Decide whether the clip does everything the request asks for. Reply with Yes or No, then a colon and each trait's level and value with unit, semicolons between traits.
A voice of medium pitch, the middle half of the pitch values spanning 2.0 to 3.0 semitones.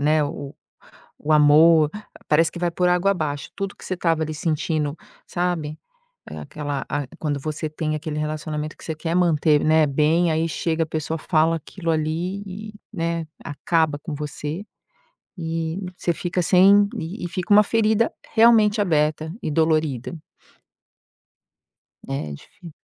Yes: medium, 160 Hz; narrow, 2.6 semitones